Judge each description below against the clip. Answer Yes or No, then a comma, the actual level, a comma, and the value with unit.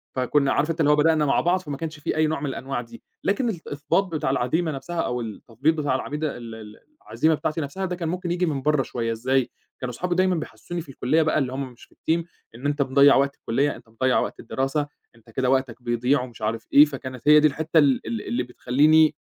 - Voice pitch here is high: No, medium, 140 Hz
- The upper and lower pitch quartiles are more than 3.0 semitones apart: Yes, average, 3.8 semitones